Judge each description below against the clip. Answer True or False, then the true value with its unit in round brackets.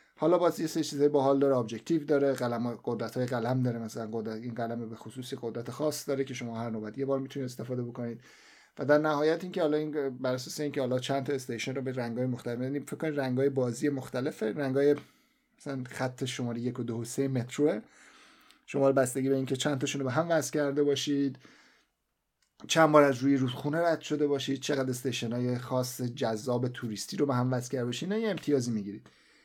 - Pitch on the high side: False (135 Hz)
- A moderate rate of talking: False (210 wpm)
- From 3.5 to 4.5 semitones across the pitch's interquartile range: False (3.1 semitones)